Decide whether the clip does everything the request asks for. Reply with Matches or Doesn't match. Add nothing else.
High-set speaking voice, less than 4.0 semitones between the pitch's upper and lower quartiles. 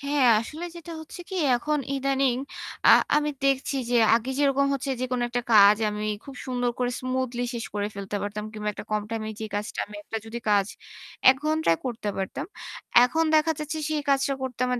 Doesn't match